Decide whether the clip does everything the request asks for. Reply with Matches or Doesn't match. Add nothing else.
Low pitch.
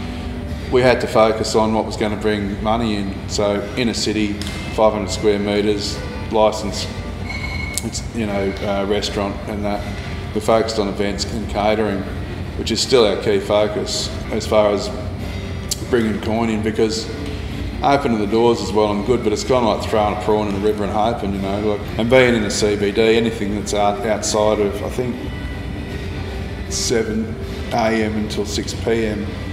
Matches